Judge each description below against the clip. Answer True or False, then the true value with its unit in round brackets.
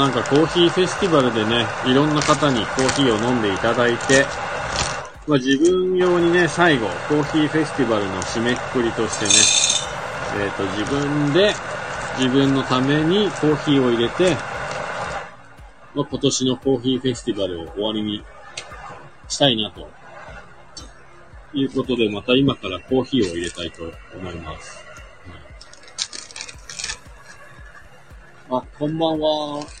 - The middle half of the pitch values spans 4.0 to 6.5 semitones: True (5.2 semitones)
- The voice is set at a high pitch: False (130 Hz)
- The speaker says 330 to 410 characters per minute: False (290 characters per minute)